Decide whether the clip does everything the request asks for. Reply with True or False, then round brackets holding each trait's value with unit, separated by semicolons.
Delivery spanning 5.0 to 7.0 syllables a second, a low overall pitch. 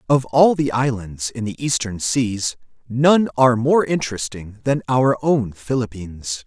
False (4.4 syllables/s; 125 Hz)